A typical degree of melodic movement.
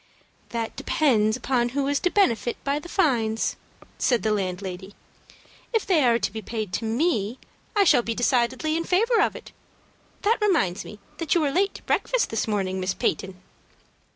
No: wide, 7.1 semitones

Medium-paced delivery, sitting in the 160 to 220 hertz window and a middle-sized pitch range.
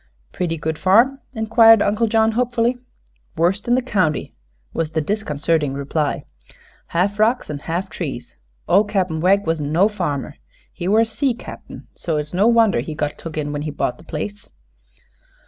No: average, 170 wpm; medium, 185 Hz; wide, 6.2 semitones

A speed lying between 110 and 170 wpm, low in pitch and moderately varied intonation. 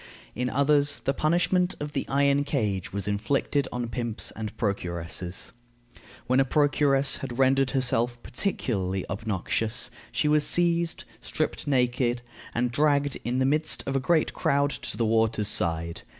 Yes: average, 150 wpm; low, 130 Hz; average, 4.3 semitones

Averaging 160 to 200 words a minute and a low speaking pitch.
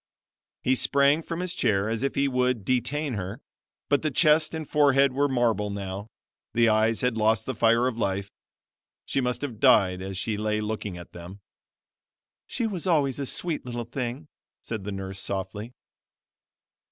Yes: average, 170 wpm; low, 120 Hz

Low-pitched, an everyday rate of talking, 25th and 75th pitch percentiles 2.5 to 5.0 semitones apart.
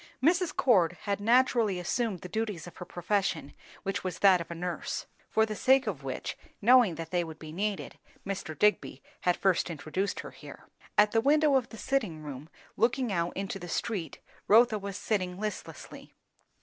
No: high, 195 Hz; average, 180 wpm; average, 4.5 semitones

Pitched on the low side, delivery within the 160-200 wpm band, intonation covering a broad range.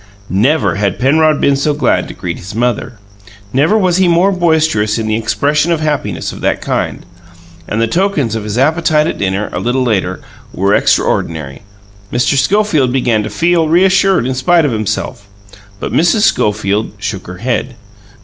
Yes: low, 130 Hz; average, 170 wpm; wide, 7.1 semitones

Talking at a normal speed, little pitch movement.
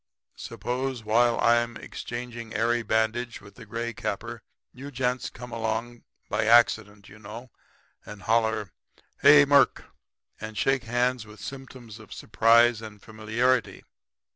No: slow, 130 wpm; narrow, 1.9 semitones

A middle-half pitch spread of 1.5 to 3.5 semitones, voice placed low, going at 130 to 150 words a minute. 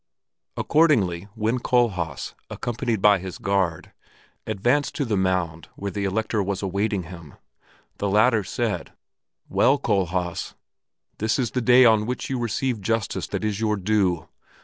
No: average, 3.9 semitones; low, 105 Hz; average, 145 wpm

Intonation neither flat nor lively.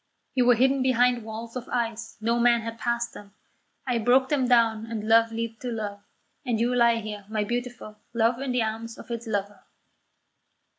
No: narrow, 1.7 semitones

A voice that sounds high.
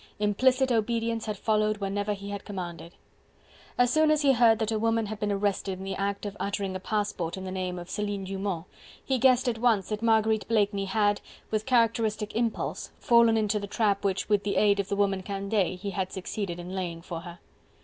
Yes: high, 205 Hz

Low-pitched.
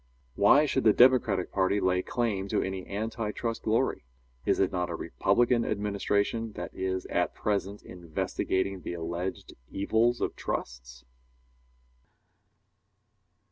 Yes: low, 100 Hz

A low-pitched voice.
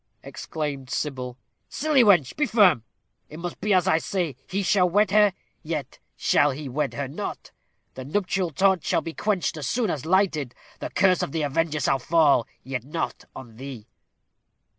No: medium, 160 Hz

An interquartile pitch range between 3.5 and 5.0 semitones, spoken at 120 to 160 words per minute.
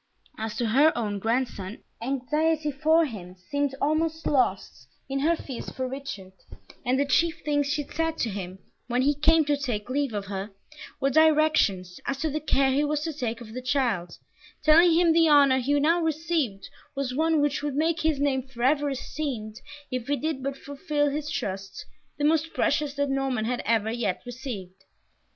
No: average, 4.5 semitones; average, 180 wpm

